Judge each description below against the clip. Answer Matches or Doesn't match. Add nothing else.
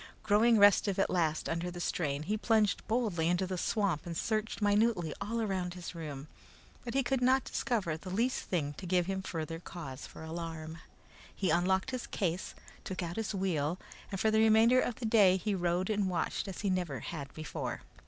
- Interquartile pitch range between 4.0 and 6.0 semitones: Matches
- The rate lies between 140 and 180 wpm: Doesn't match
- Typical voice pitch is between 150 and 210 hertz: Matches